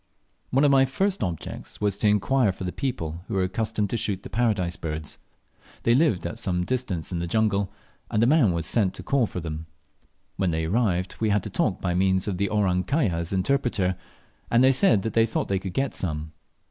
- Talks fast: Yes, fast, 210 wpm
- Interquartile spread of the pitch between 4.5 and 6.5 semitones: Yes, average, 4.8 semitones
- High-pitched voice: No, low, 100 Hz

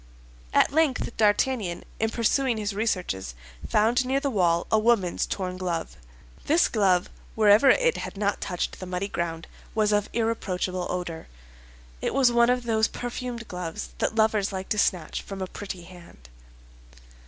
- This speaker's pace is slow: No, average, 155 wpm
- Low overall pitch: No, high, 205 Hz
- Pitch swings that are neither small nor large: Yes, average, 4.5 semitones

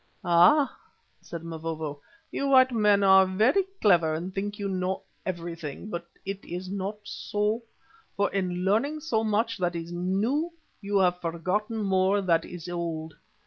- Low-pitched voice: No, high, 190 Hz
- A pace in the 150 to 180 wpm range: Yes, average, 155 wpm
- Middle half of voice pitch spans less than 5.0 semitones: Yes, average, 3.3 semitones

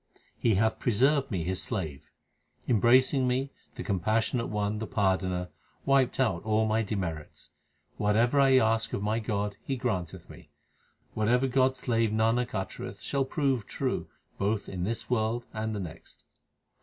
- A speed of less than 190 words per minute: Yes, average, 155 wpm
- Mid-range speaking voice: No, low, 110 Hz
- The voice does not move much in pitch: No, average, 3.7 semitones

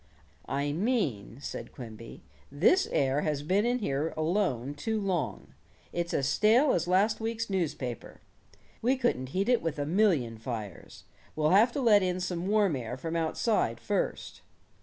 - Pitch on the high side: No, medium, 170 Hz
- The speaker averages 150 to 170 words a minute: Yes, average, 160 wpm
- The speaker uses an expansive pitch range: Yes, wide, 7.3 semitones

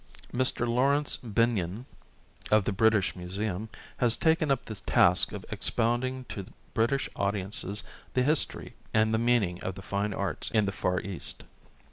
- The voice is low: Yes, low, 110 Hz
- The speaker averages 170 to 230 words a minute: No, average, 150 wpm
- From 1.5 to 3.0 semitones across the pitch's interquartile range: No, average, 3.7 semitones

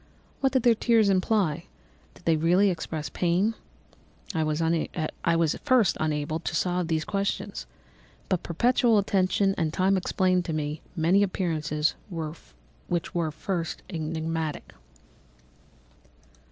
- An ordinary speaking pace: No, slow, 125 wpm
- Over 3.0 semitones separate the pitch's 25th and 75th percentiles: Yes, average, 3.6 semitones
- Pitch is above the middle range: No, medium, 170 Hz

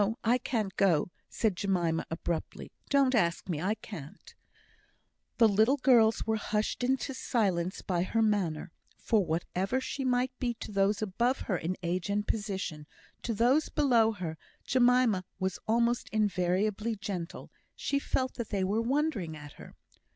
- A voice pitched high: Yes, high, 210 Hz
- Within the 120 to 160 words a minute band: Yes, average, 150 wpm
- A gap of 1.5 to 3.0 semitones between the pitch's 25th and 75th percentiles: No, average, 4.8 semitones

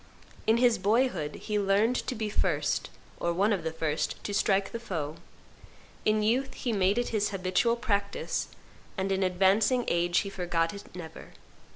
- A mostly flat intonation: No, average, 3.6 semitones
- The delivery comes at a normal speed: Yes, average, 170 wpm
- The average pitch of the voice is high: Yes, high, 200 Hz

